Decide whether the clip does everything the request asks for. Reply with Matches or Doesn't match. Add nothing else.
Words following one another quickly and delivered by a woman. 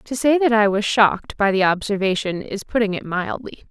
Matches